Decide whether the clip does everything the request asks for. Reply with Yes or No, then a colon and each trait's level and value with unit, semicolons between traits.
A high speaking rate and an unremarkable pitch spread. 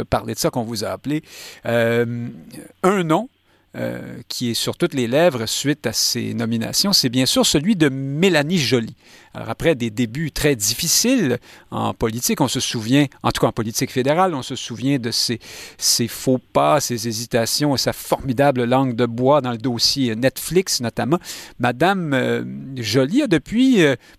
No: average, 180 wpm; average, 4.2 semitones